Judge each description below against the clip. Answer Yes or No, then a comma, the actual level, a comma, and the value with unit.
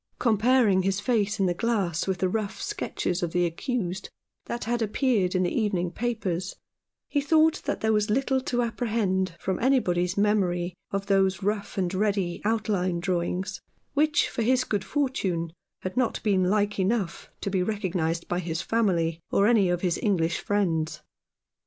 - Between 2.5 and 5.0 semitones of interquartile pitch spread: Yes, average, 4.1 semitones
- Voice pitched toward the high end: Yes, high, 195 Hz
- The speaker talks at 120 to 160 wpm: No, average, 170 wpm